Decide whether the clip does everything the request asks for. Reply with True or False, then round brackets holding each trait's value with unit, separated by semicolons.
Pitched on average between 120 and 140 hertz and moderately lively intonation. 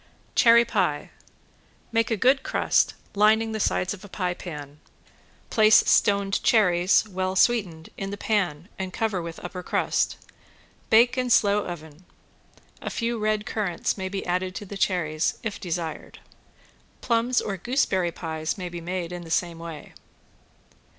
False (190 Hz; 3.9 semitones)